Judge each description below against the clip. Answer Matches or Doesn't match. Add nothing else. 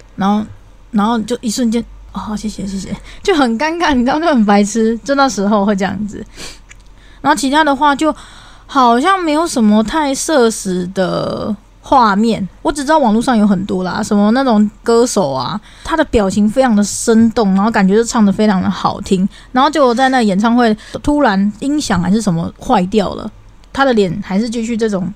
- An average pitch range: Matches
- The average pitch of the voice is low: Doesn't match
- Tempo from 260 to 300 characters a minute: Matches